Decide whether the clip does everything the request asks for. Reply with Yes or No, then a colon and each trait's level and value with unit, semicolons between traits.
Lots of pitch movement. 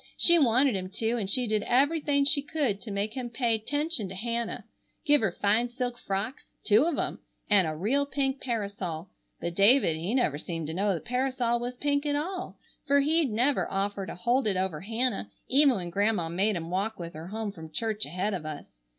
Yes: wide, 5.8 semitones